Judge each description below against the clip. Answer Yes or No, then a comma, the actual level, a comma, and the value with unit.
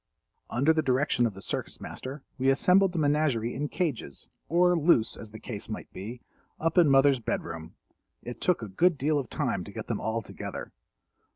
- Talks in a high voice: No, low, 135 Hz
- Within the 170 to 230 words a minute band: Yes, average, 195 wpm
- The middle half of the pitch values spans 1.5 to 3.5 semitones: No, wide, 5.5 semitones